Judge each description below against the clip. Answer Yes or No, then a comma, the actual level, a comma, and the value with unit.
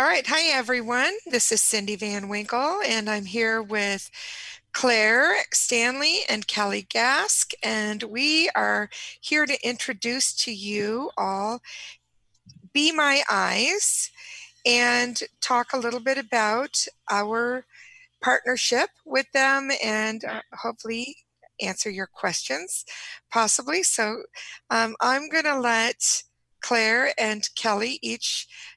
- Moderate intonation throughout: Yes, average, 4.2 semitones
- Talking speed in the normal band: No, slow, 120 wpm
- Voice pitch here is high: Yes, high, 245 Hz